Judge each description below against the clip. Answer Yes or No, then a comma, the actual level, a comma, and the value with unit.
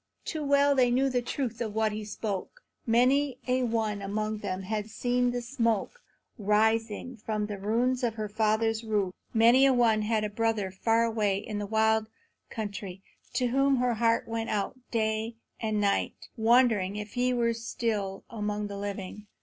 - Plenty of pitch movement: No, narrow, 2.5 semitones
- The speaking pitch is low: No, high, 220 Hz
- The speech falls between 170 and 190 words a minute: Yes, average, 175 wpm